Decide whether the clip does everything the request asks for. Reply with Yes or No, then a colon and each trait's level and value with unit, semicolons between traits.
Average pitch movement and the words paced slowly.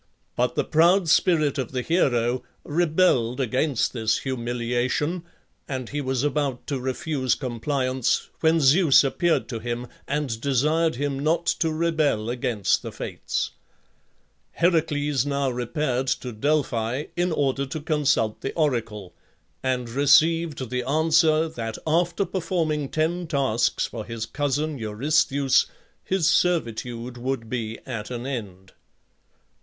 Yes: average, 4.4 semitones; slow, 130 wpm